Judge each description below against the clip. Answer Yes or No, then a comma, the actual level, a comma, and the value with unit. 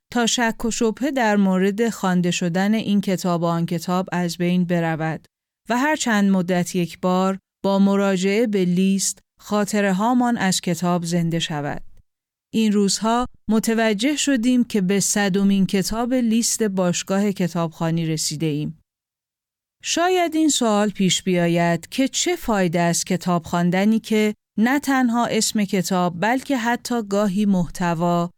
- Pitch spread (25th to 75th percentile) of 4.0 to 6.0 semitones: Yes, average, 4.3 semitones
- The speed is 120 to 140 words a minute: Yes, average, 135 wpm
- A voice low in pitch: No, high, 195 Hz